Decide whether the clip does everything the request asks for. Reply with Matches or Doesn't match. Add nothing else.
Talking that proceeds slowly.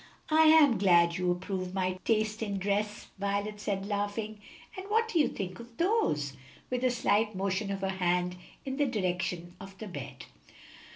Doesn't match